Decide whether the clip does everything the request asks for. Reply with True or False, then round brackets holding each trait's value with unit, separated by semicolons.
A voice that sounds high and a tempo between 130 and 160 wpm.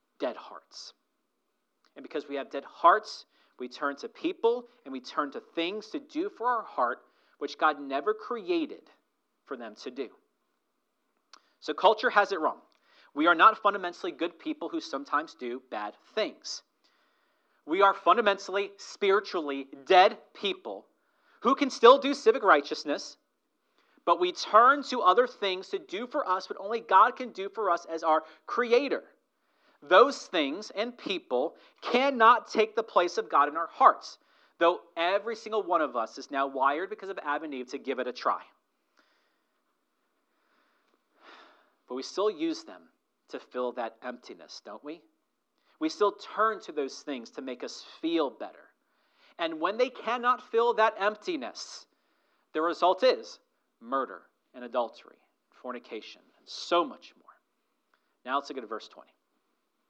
True (210 Hz; 155 wpm)